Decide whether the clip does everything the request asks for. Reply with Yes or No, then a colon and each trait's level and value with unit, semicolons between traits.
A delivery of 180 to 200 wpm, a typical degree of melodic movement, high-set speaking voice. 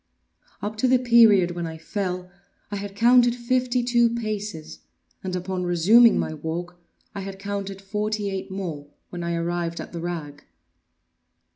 No: average, 150 wpm; average, 4.0 semitones; high, 195 Hz